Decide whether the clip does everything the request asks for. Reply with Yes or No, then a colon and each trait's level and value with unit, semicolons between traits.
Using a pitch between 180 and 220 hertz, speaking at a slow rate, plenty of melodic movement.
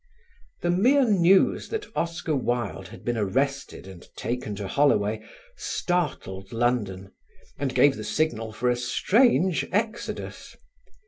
No: low, 130 Hz; slow, 125 wpm; wide, 8.2 semitones